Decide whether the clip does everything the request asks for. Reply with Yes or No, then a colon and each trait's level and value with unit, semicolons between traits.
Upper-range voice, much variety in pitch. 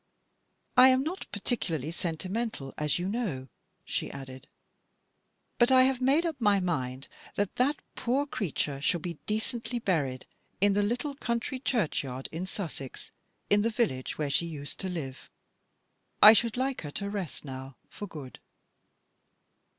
Yes: high, 195 Hz; wide, 8.6 semitones